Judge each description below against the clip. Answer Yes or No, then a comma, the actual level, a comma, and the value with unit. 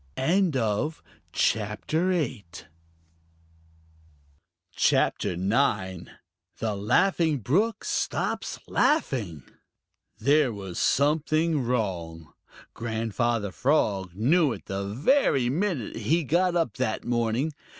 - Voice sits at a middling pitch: No, low, 120 Hz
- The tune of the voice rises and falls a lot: Yes, wide, 7.3 semitones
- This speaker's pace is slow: Yes, slow, 80 wpm